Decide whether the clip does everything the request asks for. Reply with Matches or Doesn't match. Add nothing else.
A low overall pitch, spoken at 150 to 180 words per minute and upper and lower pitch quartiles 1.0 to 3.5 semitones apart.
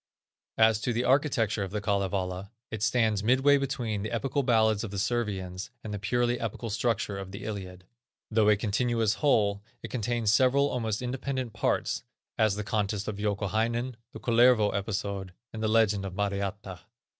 Matches